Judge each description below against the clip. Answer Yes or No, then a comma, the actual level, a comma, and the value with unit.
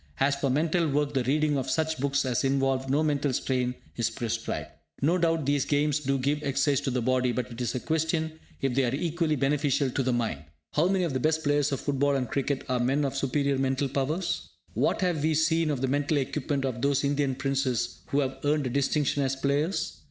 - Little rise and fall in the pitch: Yes, narrow, 2.3 semitones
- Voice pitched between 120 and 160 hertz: Yes, medium, 140 Hz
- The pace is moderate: No, fast, 220 wpm